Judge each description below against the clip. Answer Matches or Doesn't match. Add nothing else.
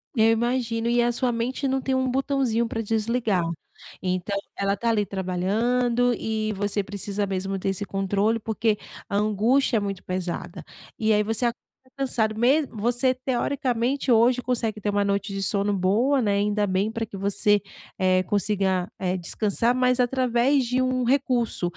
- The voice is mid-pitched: Doesn't match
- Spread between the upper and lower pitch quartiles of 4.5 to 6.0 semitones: Doesn't match